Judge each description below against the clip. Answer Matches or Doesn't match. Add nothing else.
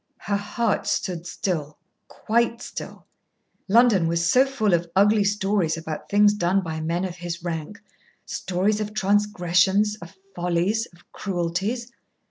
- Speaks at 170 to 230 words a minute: Doesn't match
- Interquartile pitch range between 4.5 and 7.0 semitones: Doesn't match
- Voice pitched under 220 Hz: Matches